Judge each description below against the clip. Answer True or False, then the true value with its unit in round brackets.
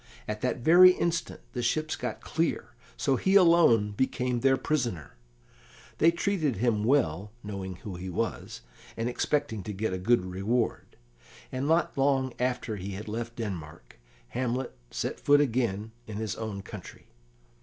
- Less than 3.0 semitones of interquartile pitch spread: False (5.1 semitones)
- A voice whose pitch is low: True (120 Hz)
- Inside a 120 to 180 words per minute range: True (155 wpm)